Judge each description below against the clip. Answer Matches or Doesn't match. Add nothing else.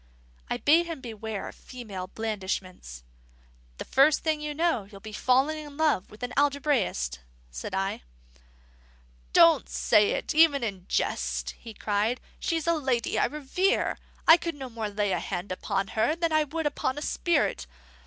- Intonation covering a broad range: Matches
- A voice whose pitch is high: Matches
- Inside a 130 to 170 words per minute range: Matches